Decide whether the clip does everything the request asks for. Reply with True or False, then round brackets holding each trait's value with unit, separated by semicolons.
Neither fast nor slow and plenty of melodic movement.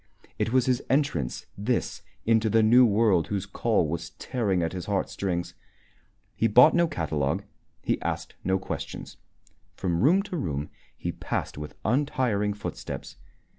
True (145 wpm; 6.2 semitones)